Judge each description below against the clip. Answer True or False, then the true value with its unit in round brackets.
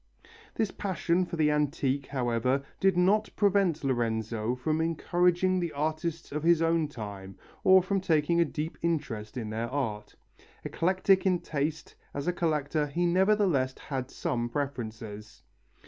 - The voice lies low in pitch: False (150 Hz)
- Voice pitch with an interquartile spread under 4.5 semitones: False (5.5 semitones)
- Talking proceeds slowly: False (145 wpm)